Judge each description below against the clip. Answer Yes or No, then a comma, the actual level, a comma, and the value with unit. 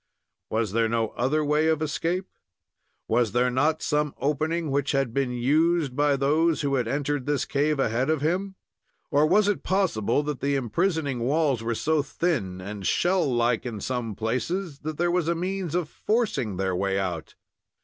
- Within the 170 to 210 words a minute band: Yes, average, 180 wpm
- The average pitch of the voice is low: No, medium, 145 Hz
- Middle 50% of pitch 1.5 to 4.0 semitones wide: No, average, 5.0 semitones